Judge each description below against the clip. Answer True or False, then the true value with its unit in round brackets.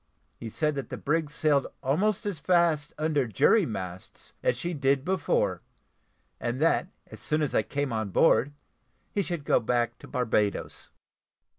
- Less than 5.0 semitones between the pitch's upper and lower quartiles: False (5.3 semitones)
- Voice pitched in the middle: True (145 Hz)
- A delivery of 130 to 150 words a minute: False (160 wpm)